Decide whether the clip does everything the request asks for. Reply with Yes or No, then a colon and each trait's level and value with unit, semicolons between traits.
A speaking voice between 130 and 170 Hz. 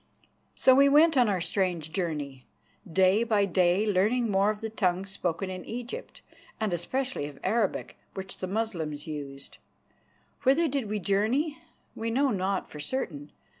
No: high, 200 Hz